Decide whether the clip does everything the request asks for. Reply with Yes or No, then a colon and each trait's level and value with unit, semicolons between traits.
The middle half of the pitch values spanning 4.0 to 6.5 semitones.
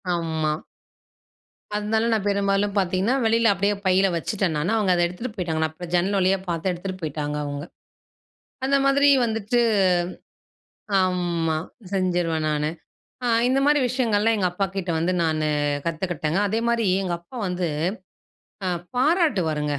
Yes: average, 4.6 semitones